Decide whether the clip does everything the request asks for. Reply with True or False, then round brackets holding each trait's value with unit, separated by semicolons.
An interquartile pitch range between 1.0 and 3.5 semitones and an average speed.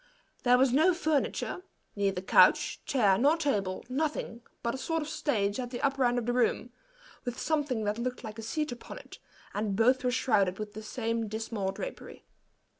False (4.3 semitones; 190 wpm)